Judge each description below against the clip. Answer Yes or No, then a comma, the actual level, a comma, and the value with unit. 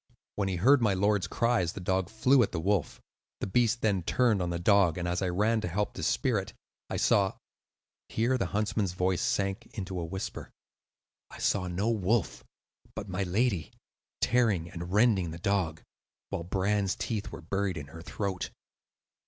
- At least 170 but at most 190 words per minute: Yes, average, 175 wpm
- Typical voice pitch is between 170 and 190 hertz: No, very low, 95 Hz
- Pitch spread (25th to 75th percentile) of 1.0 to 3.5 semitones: Yes, average, 3.1 semitones